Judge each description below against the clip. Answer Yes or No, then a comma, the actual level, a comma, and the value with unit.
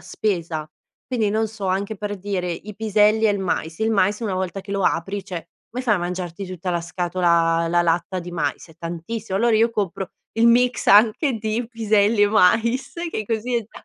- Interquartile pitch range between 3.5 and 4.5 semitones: Yes, average, 3.9 semitones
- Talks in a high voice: Yes, high, 200 Hz